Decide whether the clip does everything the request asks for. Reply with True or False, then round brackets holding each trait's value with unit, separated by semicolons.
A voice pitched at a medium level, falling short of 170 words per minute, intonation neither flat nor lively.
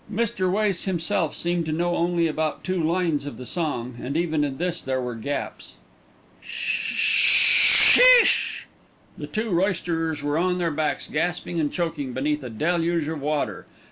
True (165 Hz; 155 wpm; 3.2 semitones)